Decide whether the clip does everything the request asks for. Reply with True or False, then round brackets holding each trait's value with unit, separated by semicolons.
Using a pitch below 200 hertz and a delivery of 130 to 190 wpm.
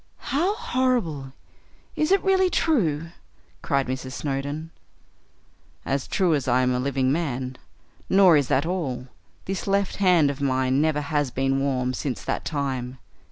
True (140 Hz; 150 wpm)